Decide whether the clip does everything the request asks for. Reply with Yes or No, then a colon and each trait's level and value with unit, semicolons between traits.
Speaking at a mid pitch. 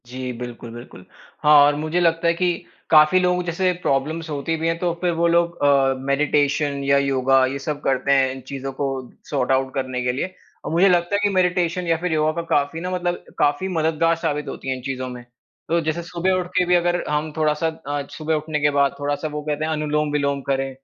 Yes: medium, 150 Hz